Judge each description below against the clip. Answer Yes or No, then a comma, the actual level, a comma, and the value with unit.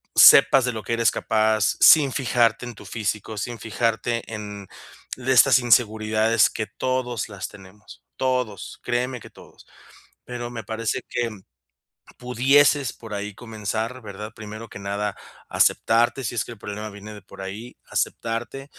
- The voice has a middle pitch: No, low, 115 Hz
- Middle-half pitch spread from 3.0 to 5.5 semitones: No, narrow, 2.4 semitones